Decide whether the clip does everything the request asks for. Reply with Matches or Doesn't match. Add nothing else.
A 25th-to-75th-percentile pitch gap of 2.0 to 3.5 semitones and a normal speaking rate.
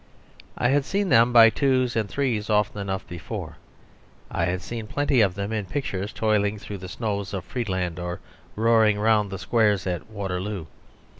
Matches